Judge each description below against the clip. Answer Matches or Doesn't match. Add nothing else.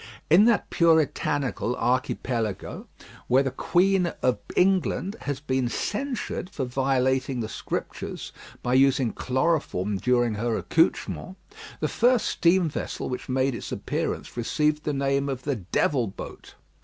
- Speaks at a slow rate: Matches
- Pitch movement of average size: Matches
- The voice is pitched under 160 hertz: Matches